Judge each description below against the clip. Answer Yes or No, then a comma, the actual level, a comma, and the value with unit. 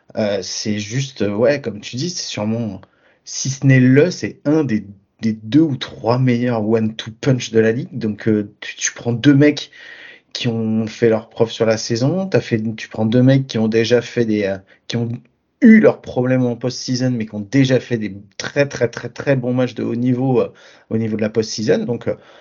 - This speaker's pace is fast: Yes, fast, 225 wpm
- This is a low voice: Yes, low, 120 Hz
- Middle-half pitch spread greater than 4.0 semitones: No, average, 3.0 semitones